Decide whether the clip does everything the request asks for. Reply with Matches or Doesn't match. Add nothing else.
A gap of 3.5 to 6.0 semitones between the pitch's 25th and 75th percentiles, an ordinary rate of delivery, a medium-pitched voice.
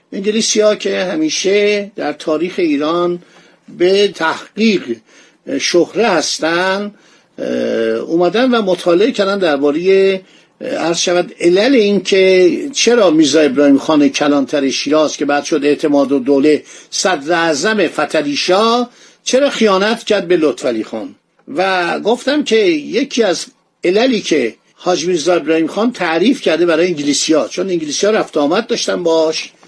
Matches